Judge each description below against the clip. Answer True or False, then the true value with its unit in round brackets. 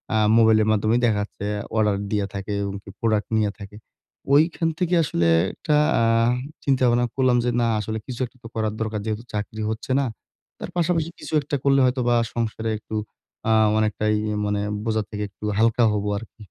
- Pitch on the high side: False (110 Hz)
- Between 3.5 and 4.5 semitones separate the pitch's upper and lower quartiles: False (2.8 semitones)